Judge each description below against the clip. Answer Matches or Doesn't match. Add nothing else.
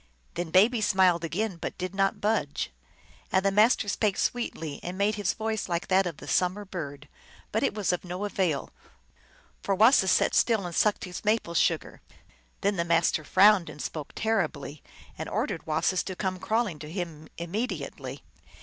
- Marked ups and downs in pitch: Doesn't match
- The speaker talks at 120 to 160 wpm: Doesn't match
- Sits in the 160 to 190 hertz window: Matches